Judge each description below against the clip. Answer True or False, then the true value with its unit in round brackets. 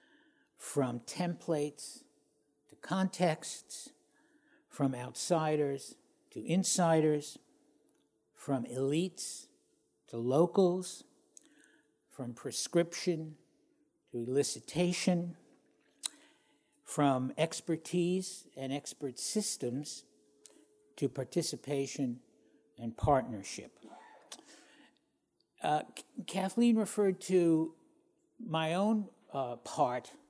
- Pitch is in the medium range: True (165 Hz)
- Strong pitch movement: True (5.8 semitones)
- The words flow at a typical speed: False (65 wpm)